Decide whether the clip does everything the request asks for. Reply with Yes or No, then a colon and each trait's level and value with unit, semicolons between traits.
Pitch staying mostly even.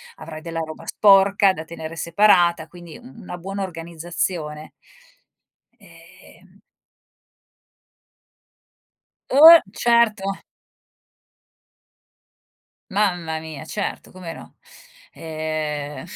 No: average, 3.5 semitones